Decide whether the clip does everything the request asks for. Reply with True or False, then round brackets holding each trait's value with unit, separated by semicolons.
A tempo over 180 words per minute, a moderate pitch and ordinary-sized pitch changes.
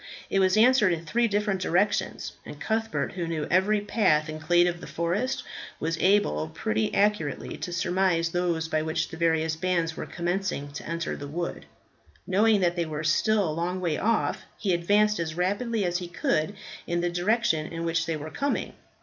True (190 wpm; 175 Hz; 3.8 semitones)